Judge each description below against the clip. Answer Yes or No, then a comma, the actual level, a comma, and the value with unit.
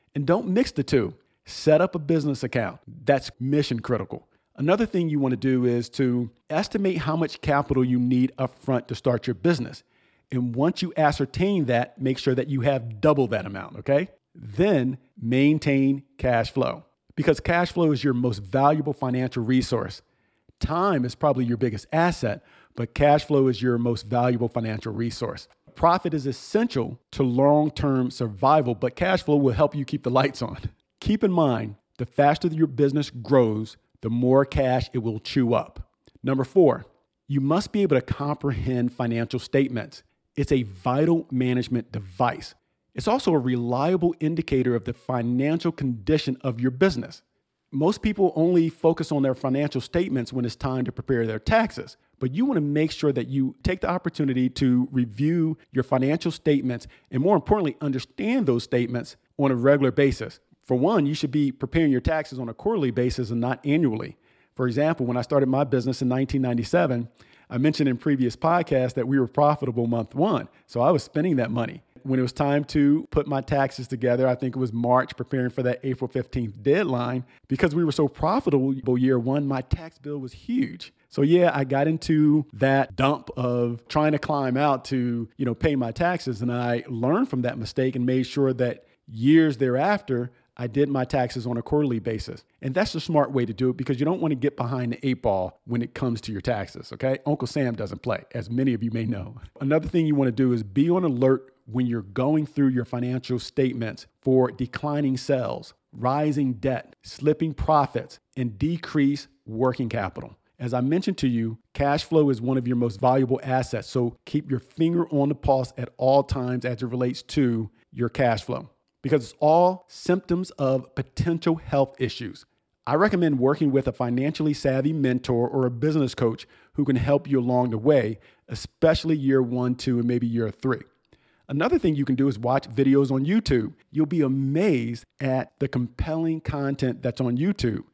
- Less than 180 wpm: No, average, 190 wpm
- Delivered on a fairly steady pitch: No, average, 3.1 semitones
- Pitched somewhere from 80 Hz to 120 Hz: No, low, 130 Hz